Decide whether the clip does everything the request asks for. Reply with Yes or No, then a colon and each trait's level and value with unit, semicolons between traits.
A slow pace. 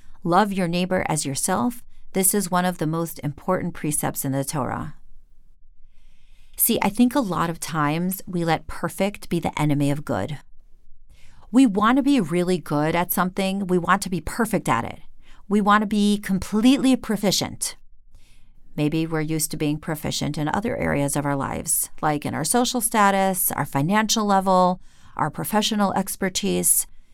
No: average, 165 wpm